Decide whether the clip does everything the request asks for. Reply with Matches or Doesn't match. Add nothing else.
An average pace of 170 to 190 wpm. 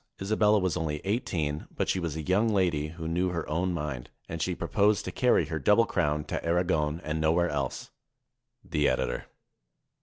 Matches